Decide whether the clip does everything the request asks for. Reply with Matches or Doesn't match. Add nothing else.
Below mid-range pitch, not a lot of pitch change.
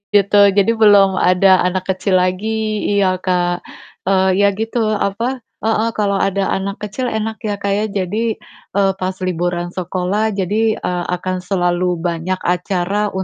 Doesn't match